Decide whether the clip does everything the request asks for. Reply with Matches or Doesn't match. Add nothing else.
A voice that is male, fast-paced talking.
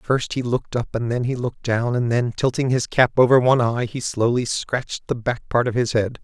Matches